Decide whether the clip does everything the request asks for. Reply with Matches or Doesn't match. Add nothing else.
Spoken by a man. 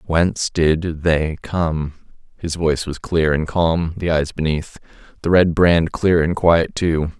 Matches